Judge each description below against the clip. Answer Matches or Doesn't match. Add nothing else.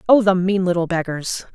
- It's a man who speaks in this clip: Doesn't match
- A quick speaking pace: Doesn't match